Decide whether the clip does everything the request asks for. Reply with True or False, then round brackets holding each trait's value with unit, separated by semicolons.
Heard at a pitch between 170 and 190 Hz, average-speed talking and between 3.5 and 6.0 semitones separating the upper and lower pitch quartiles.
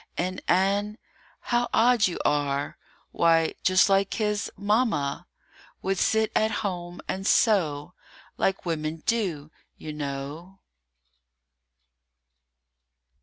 False (185 Hz; 100 wpm; 5.2 semitones)